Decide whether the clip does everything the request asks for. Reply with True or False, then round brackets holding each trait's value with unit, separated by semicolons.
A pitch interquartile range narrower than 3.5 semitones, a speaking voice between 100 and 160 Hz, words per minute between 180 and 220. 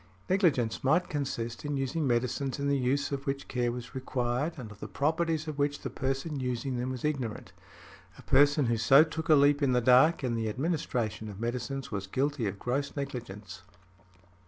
True (3.1 semitones; 135 Hz; 190 wpm)